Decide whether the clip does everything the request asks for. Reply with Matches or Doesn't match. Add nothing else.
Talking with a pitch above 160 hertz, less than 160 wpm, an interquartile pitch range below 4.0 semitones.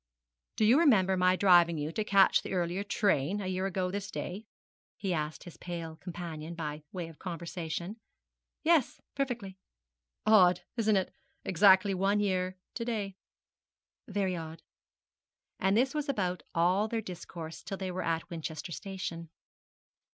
Matches